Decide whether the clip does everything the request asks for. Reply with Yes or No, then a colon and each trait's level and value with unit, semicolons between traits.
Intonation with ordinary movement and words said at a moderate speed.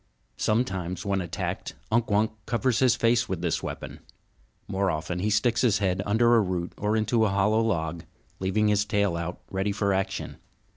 Yes: average, 3.1 semitones; average, 180 wpm